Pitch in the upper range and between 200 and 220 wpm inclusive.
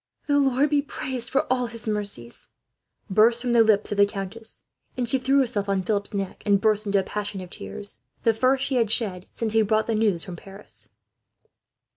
Yes: high, 215 Hz; fast, 205 wpm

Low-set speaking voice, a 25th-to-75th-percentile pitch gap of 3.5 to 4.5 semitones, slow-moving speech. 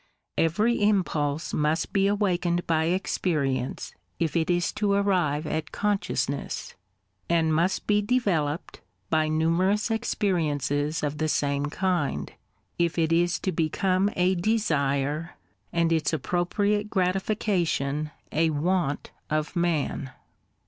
No: medium, 170 Hz; average, 3.9 semitones; slow, 115 wpm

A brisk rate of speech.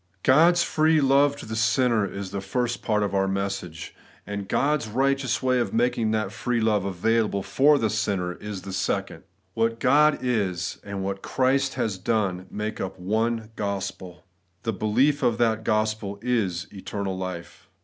No: average, 165 wpm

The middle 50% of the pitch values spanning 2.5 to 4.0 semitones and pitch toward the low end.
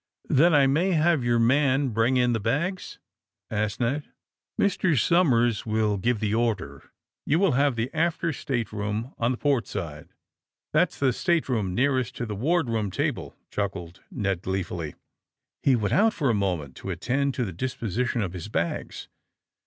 No: average, 5.3 semitones; low, 120 Hz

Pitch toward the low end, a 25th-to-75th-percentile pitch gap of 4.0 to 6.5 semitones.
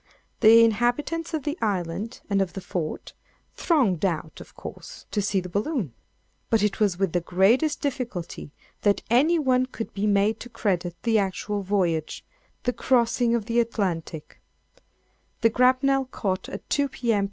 No: high, 220 Hz; average, 4.8 semitones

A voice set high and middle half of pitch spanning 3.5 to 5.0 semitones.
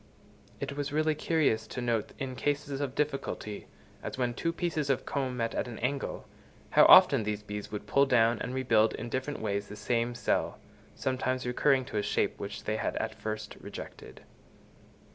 No: low, 125 Hz; average, 4.1 semitones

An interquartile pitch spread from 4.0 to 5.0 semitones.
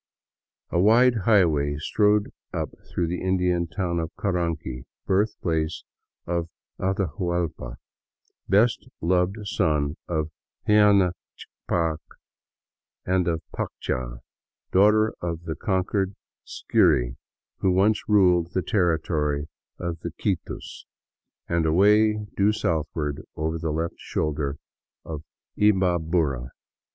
No: average, 3.6 semitones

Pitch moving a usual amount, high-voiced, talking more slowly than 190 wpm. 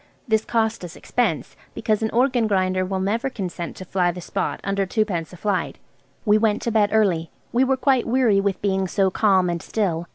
No: average, 3.1 semitones; high, 200 Hz; average, 200 wpm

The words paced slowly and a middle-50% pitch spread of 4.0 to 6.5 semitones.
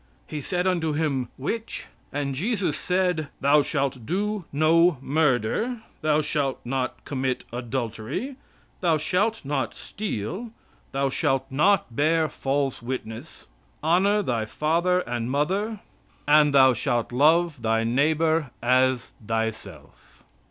Yes: slow, 120 wpm; average, 5.0 semitones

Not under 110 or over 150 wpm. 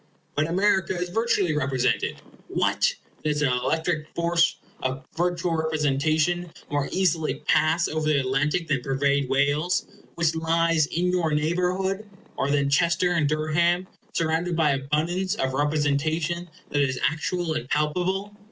Yes: slow, 135 wpm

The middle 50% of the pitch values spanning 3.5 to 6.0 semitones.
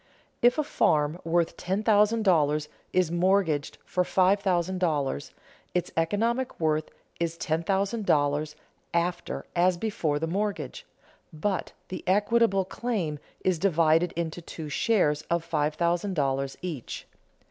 Yes: average, 4.0 semitones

